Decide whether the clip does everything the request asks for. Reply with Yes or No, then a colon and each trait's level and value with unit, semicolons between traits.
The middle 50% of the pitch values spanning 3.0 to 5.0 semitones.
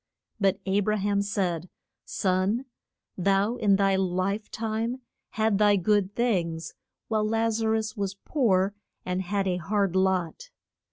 No: narrow, 2.5 semitones